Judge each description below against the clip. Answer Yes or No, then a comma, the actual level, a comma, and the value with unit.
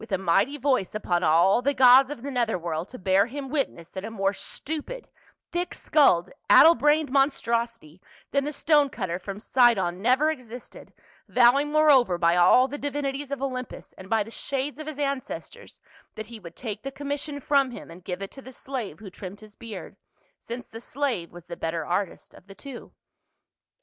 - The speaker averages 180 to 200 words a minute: Yes, average, 190 wpm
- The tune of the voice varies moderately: No, wide, 6.5 semitones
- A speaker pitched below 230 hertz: No, high, 240 Hz